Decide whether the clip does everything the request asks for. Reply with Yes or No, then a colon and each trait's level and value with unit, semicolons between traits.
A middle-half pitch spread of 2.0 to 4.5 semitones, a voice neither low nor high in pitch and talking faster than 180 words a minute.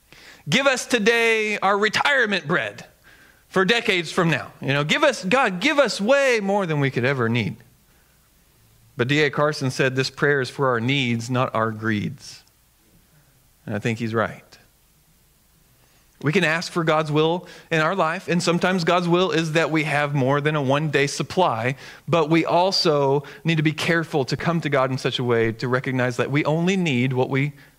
No: average, 5.2 semitones; medium, 150 Hz; average, 190 wpm